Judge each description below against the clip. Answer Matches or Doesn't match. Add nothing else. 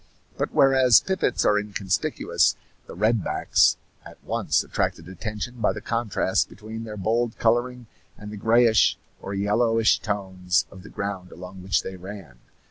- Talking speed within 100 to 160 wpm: Matches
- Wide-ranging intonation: Doesn't match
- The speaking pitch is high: Doesn't match